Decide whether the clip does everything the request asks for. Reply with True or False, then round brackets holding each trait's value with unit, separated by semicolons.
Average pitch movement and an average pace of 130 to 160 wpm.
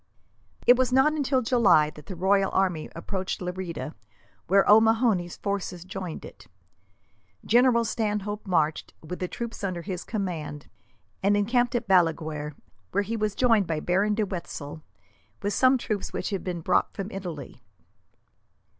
True (4.2 semitones; 145 wpm)